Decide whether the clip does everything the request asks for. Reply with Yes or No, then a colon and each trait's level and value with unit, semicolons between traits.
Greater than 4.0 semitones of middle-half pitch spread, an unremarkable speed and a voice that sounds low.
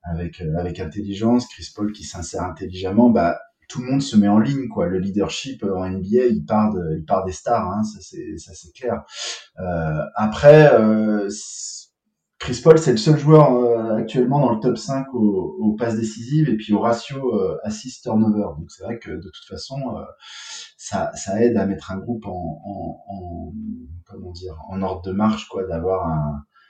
Yes: average, 4.4 semitones; average, 195 wpm; low, 105 Hz